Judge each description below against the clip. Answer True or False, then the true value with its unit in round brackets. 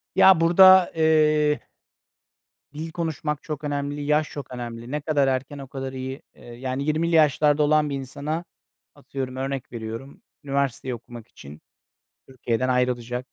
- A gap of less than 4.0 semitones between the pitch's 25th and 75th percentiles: True (3.0 semitones)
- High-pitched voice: False (140 Hz)